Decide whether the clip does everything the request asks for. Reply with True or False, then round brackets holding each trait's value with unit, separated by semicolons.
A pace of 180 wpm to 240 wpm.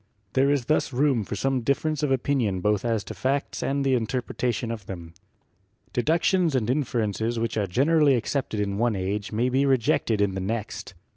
True (195 wpm)